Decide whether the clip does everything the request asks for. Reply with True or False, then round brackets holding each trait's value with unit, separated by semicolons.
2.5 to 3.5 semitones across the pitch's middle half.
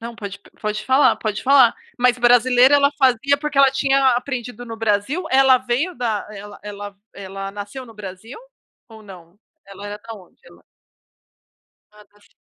False (4.2 semitones)